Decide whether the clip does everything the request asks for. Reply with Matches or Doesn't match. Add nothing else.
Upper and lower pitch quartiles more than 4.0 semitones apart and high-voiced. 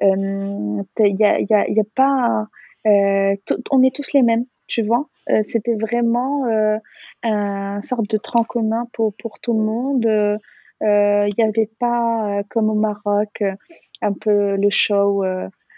Doesn't match